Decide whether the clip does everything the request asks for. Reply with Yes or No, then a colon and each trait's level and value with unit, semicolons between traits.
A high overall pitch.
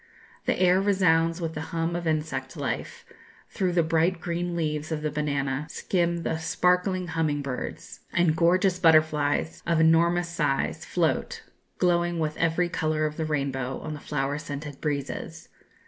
No: medium, 160 Hz